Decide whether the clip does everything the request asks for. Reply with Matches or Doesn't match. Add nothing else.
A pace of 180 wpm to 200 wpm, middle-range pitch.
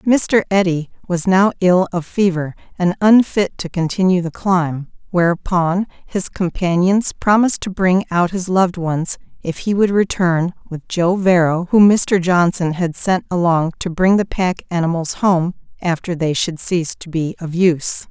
Doesn't match